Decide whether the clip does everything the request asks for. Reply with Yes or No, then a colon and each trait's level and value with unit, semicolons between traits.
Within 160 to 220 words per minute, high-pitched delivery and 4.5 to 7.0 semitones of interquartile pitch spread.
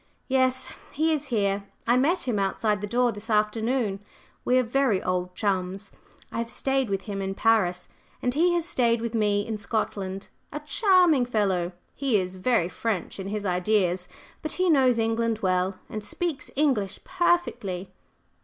Yes: average, 165 wpm; high, 220 Hz; average, 4.9 semitones